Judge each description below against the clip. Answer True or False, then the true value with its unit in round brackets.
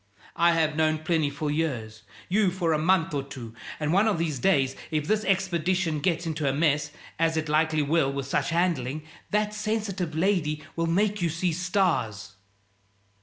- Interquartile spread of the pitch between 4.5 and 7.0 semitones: False (3.6 semitones)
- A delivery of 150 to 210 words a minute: True (175 wpm)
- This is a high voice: False (160 Hz)